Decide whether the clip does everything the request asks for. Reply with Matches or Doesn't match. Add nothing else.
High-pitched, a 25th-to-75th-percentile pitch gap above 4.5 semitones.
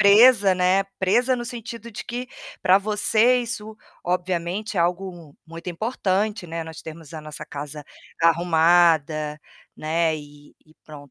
Doesn't match